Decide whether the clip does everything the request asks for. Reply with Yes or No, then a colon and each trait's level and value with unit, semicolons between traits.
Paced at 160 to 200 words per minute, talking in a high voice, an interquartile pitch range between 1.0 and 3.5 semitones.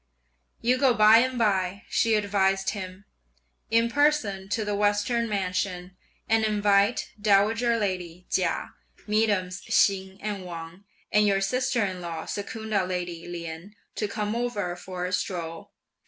No: average, 140 wpm; high, 200 Hz; average, 3.1 semitones